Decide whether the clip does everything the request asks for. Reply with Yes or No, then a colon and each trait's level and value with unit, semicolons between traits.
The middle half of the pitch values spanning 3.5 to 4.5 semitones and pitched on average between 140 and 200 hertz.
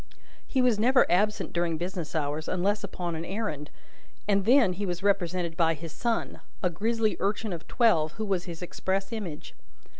Yes: average, 3.9 semitones; medium, 185 Hz